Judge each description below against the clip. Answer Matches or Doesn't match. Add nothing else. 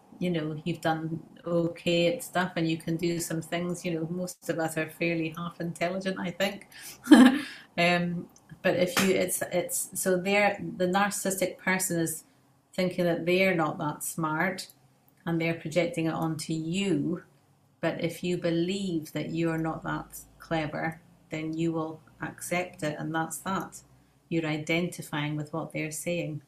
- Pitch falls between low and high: Matches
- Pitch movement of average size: Doesn't match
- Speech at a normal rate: Matches